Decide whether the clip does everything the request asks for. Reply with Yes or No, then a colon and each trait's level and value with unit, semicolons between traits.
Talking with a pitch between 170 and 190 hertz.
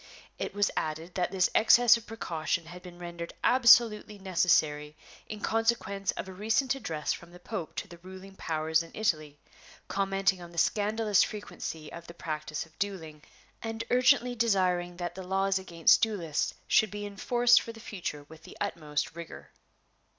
Yes: medium, 185 Hz